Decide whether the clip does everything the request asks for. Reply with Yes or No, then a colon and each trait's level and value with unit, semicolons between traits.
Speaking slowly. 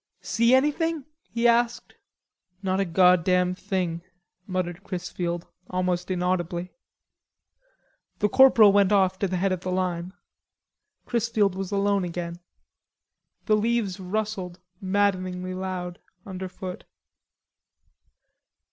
Yes: slow, 105 wpm